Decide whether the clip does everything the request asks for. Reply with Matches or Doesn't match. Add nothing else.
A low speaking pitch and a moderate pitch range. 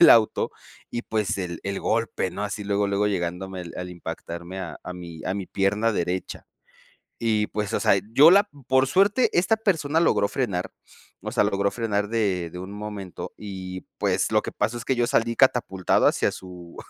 Matches